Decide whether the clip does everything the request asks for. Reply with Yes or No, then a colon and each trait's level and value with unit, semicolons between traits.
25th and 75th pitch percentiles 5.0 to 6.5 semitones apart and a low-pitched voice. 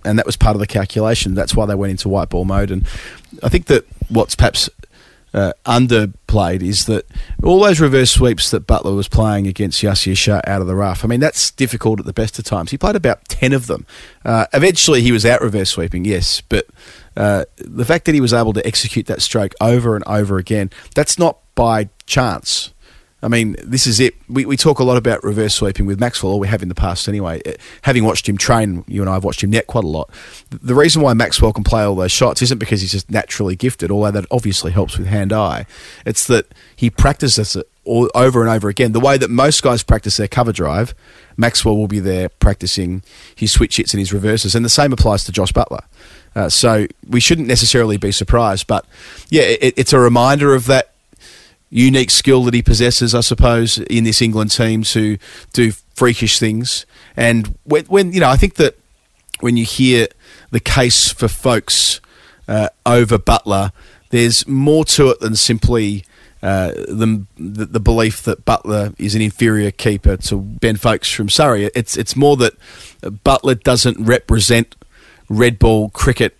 No: average, 3.3 semitones; low, 110 Hz